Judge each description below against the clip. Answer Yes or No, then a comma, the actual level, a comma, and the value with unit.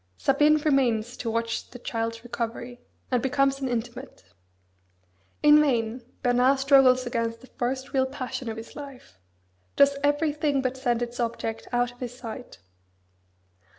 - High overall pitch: Yes, very high, 250 Hz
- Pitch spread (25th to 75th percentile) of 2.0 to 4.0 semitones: Yes, narrow, 2.5 semitones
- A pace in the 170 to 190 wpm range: No, average, 145 wpm